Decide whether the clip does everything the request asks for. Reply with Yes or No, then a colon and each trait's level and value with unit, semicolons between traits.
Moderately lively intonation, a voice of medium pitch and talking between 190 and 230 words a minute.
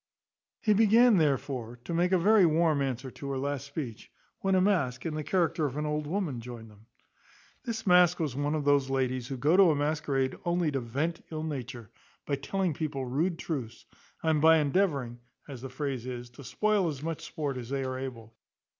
Yes: average, 4.5 semitones; medium, 145 Hz; average, 200 wpm